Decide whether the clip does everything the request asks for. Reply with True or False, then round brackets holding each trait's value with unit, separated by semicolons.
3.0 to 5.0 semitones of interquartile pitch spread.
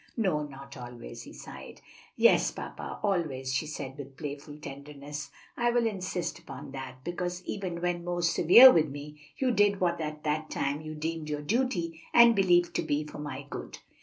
True (3.8 semitones)